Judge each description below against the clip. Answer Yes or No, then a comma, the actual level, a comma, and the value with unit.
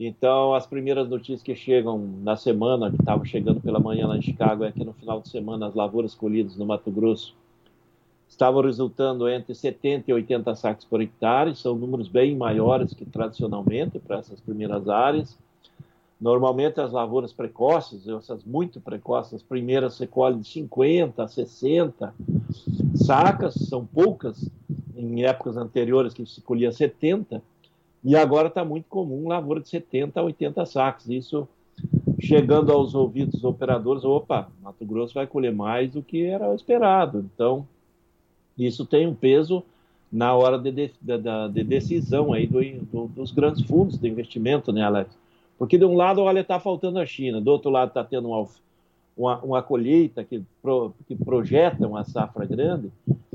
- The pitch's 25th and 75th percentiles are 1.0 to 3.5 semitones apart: No, average, 4.2 semitones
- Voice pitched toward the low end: Yes, low, 130 Hz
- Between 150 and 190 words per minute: Yes, average, 165 wpm